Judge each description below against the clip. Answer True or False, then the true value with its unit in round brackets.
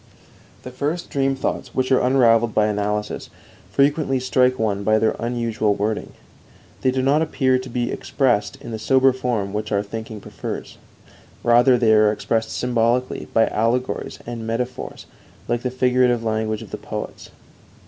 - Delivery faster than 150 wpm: True (160 wpm)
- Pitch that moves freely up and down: False (2.8 semitones)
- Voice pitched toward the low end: True (120 Hz)